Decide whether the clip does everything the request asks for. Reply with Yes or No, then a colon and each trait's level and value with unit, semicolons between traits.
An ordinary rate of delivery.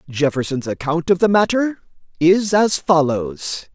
No: slow, 130 wpm